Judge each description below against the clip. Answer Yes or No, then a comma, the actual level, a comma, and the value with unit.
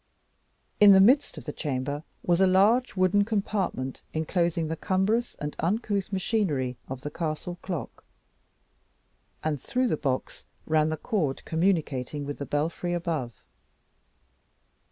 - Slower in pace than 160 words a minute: Yes, slow, 135 wpm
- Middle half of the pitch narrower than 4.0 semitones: No, average, 4.9 semitones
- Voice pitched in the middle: Yes, medium, 170 Hz